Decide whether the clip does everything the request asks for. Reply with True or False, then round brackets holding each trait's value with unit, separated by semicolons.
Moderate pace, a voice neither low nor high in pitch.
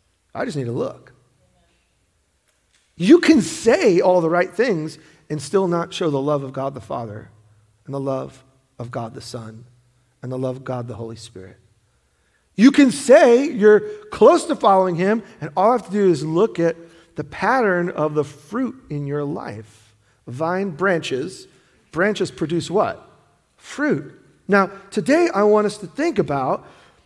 True (170 wpm; 165 Hz)